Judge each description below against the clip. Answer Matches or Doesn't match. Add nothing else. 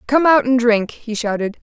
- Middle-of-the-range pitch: Doesn't match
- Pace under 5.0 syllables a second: Matches